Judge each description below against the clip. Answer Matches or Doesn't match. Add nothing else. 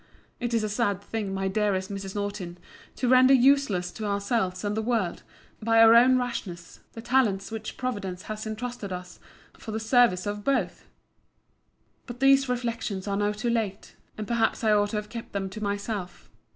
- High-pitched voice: Matches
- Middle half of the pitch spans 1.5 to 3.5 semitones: Matches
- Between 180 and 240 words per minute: Matches